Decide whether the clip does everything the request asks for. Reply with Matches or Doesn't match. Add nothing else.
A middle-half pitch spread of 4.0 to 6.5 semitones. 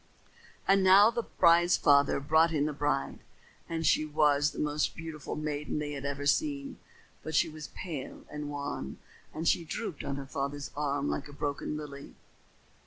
Doesn't match